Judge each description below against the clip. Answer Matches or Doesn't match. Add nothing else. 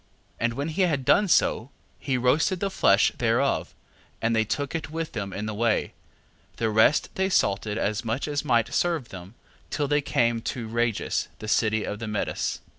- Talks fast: Doesn't match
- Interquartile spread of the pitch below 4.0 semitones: Doesn't match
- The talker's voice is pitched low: Matches